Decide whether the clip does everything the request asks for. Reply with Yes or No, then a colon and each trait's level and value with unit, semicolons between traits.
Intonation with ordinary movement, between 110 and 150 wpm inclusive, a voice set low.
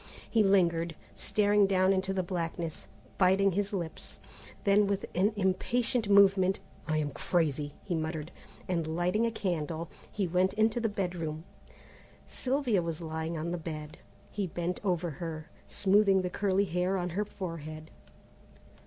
No: average, 3.3 semitones; average, 145 wpm; medium, 180 Hz